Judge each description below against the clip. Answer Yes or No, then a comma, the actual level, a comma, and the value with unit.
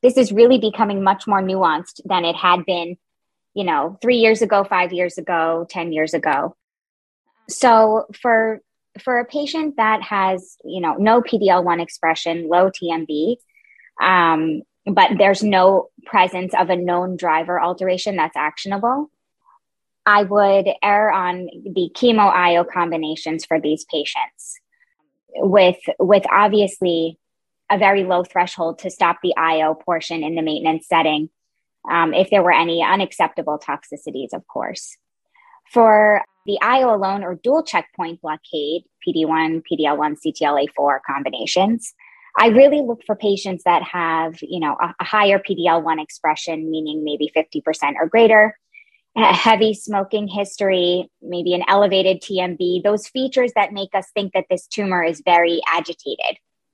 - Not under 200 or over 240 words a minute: No, average, 145 wpm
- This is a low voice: No, medium, 185 Hz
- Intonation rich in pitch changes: No, average, 4.2 semitones